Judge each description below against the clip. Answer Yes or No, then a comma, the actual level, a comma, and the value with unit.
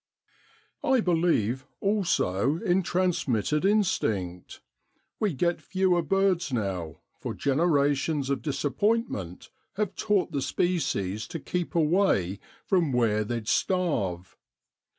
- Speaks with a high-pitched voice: No, medium, 155 Hz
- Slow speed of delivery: Yes, slow, 110 wpm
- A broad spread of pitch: Yes, wide, 8.7 semitones